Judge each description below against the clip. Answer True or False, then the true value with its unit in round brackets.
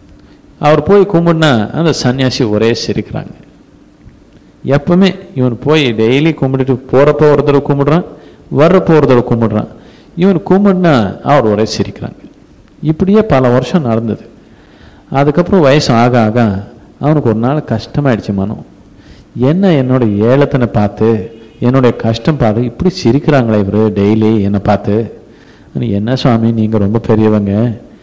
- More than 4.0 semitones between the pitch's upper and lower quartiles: True (5.3 semitones)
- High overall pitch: False (125 Hz)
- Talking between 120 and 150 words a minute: False (110 wpm)